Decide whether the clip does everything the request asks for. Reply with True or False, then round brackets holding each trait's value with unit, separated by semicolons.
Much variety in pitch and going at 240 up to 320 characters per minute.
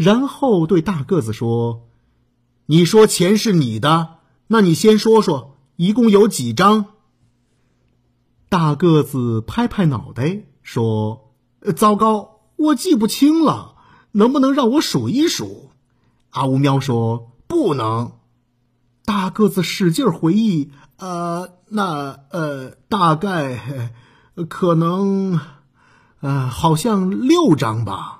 False (8.9 semitones; 155 characters per minute)